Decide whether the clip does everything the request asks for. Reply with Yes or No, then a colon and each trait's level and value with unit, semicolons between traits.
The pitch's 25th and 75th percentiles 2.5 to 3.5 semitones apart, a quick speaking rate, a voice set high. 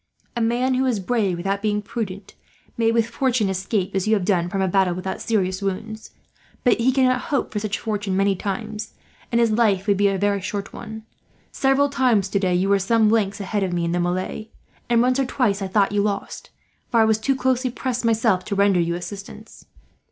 Yes: average, 3.1 semitones; fast, 215 wpm; high, 210 Hz